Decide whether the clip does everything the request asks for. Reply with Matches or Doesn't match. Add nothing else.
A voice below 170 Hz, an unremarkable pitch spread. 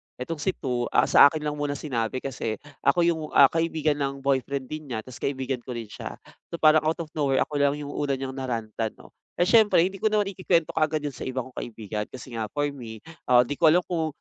Matches